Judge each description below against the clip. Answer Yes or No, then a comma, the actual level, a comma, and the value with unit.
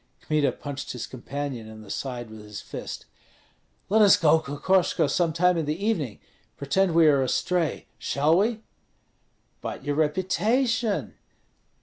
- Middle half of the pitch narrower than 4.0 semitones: No, average, 5.2 semitones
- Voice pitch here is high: No, medium, 155 Hz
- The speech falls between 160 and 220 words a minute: No, average, 140 wpm